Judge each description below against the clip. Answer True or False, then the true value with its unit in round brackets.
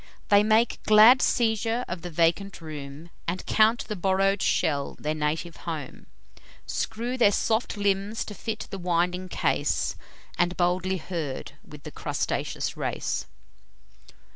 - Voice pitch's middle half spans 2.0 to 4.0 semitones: False (4.4 semitones)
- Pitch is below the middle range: False (185 Hz)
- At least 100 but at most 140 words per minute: True (135 wpm)